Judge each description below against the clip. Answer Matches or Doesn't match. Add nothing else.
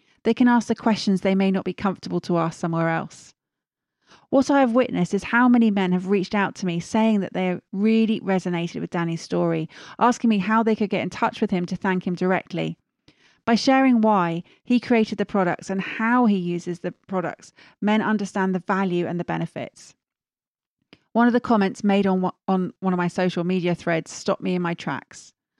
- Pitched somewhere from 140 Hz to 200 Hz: Matches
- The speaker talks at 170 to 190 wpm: Doesn't match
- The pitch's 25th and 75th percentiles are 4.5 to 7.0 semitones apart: Doesn't match